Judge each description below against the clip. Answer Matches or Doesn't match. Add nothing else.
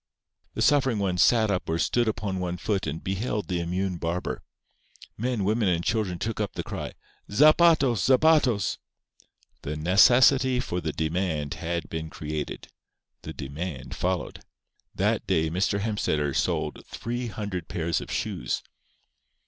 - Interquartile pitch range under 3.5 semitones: Doesn't match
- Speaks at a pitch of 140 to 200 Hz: Doesn't match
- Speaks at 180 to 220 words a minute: Doesn't match